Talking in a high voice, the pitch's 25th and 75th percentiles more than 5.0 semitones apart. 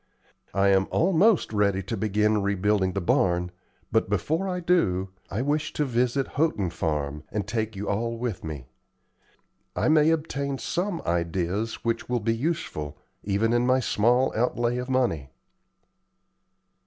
No: low, 110 Hz; wide, 5.6 semitones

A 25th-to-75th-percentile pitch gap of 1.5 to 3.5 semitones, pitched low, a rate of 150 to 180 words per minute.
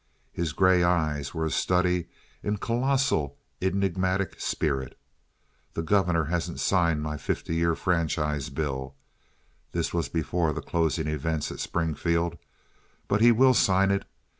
No: average, 3.2 semitones; very low, 85 Hz; slow, 135 wpm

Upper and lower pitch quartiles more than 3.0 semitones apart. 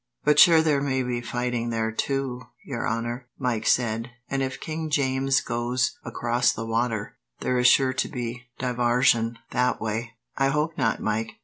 No: narrow, 2.4 semitones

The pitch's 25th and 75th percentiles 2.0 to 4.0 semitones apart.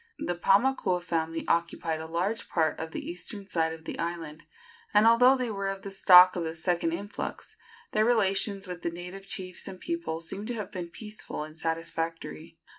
Yes: average, 3.4 semitones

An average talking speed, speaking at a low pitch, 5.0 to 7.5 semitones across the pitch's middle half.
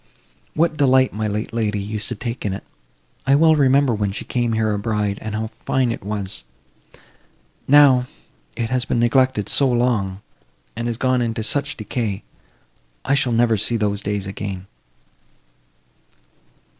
No: average, 155 wpm; low, 115 Hz; average, 3.6 semitones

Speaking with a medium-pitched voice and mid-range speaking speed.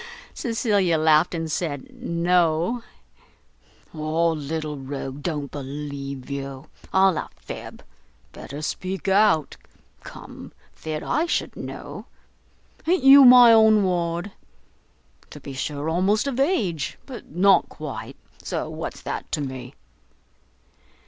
No: medium, 165 Hz; slow, 115 wpm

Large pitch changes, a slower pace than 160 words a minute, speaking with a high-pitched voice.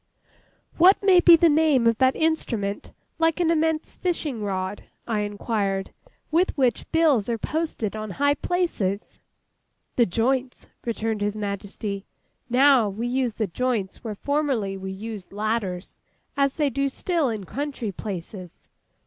Yes: wide, 6.2 semitones; average, 140 wpm; high, 235 Hz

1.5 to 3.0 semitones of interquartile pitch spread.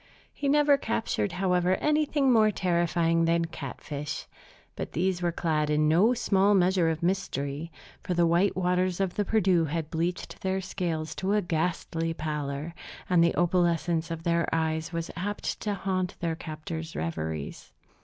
Yes: average, 2.7 semitones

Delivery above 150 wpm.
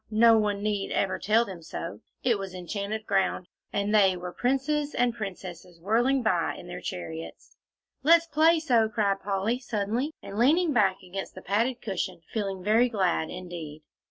Yes: average, 165 wpm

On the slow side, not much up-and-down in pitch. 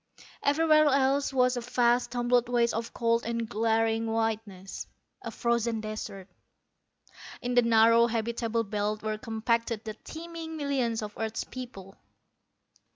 Yes: slow, 130 wpm; narrow, 1.9 semitones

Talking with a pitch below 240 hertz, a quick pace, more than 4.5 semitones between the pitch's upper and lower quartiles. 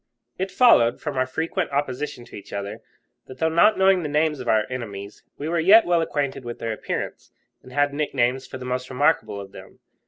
Yes: low, 135 Hz; fast, 210 wpm; average, 5.0 semitones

